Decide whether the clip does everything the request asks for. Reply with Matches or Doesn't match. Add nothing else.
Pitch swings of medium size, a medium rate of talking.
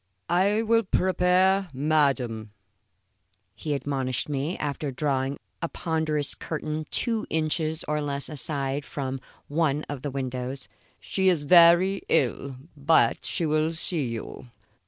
Doesn't match